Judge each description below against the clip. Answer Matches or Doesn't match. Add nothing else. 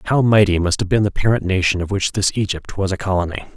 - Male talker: Matches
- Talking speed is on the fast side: Matches